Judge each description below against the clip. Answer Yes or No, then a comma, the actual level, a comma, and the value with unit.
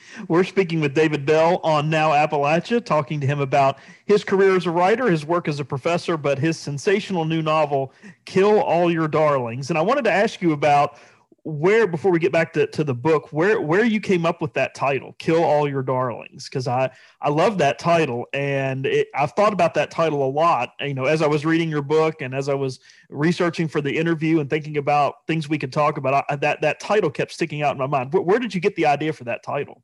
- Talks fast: Yes, fast, 235 wpm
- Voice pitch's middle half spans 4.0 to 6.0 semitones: No, average, 3.0 semitones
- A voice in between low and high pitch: Yes, medium, 155 Hz